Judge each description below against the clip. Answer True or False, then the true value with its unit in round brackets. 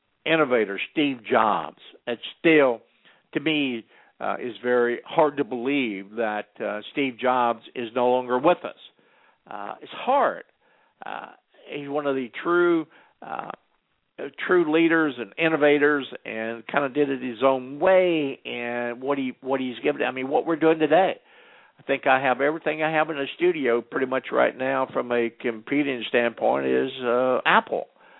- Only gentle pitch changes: False (3.7 semitones)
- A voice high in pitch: False (135 Hz)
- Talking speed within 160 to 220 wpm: True (165 wpm)